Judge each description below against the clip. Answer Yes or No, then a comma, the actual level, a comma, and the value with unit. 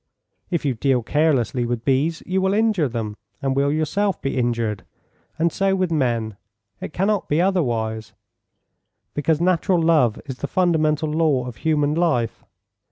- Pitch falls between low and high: Yes, medium, 150 Hz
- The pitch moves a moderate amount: No, wide, 5.7 semitones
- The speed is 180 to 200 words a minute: No, average, 155 wpm